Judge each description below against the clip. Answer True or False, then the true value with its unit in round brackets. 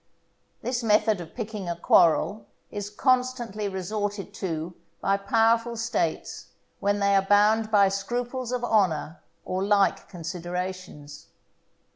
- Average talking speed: False (120 wpm)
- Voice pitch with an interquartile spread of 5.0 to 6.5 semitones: False (3.3 semitones)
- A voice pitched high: True (205 Hz)